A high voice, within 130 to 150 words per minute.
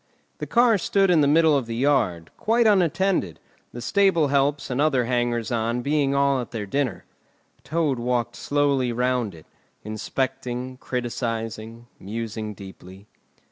No: low, 125 Hz; average, 140 wpm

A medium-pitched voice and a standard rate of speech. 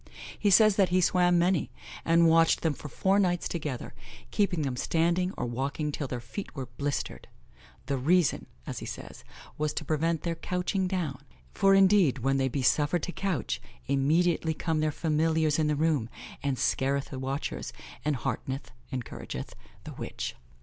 Yes: medium, 155 Hz; average, 170 wpm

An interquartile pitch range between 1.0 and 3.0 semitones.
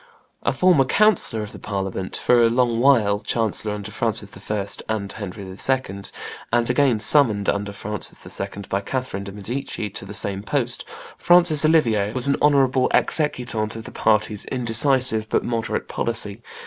No: average, 4.3 semitones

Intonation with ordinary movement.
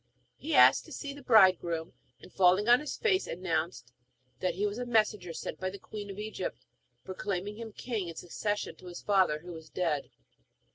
Yes: average, 3.7 semitones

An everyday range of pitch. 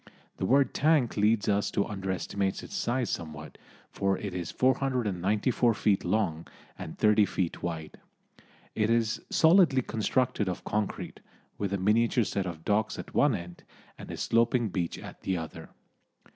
Yes: average, 4.0 semitones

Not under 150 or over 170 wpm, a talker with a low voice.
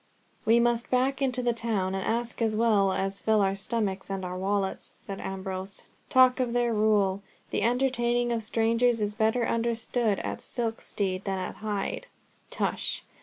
No: average, 165 wpm; high, 220 Hz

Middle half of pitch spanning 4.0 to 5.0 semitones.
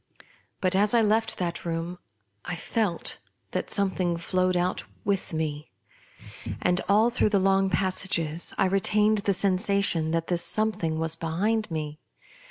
No: average, 3.3 semitones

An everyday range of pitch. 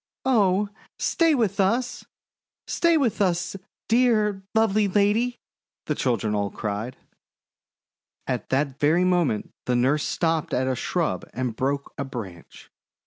No: wide, 8.7 semitones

